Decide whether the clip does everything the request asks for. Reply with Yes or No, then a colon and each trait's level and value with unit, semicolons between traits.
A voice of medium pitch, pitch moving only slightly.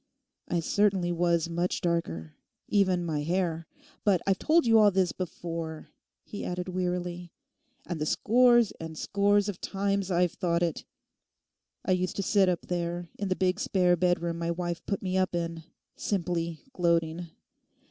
Yes: medium, 175 Hz; narrow, 2.2 semitones